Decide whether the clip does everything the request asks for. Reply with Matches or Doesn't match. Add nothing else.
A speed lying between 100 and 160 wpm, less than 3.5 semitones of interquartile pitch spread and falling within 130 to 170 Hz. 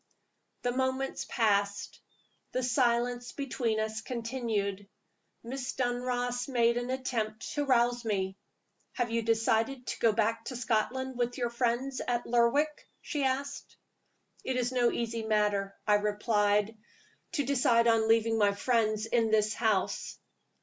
Doesn't match